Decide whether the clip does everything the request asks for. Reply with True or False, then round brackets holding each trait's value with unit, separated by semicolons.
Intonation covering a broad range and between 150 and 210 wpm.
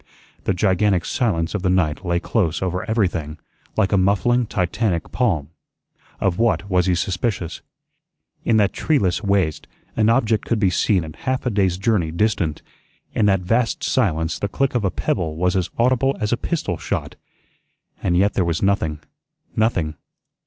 False (4.2 semitones; 165 wpm)